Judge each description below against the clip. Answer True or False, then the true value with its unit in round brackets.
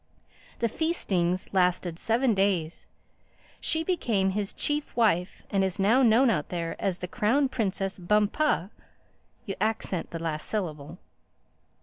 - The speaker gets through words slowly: True (125 wpm)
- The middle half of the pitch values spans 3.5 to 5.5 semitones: True (4.5 semitones)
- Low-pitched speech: False (195 Hz)